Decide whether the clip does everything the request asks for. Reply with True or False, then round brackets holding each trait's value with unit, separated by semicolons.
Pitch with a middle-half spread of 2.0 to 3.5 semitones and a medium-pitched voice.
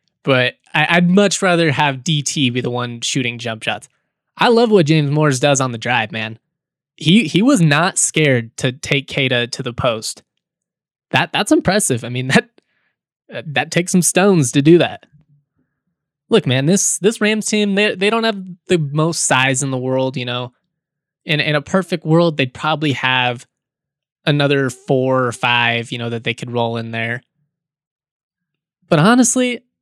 False (5.1 semitones; 150 Hz)